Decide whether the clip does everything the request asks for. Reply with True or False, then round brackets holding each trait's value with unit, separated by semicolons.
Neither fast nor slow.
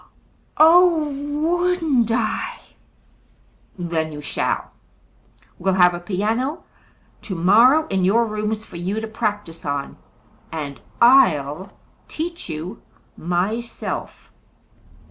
False (95 wpm)